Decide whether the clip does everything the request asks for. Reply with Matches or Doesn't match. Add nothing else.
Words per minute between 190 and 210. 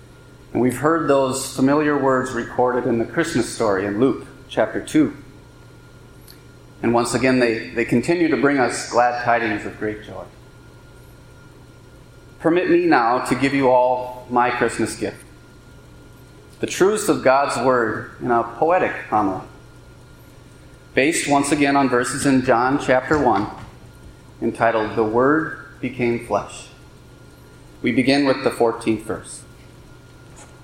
Doesn't match